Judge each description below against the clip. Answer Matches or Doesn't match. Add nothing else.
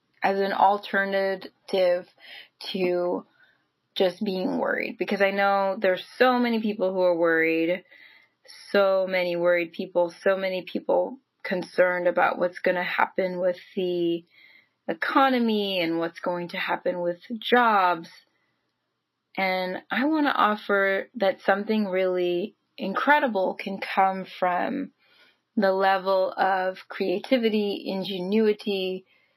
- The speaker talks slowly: Matches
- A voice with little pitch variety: Matches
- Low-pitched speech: Doesn't match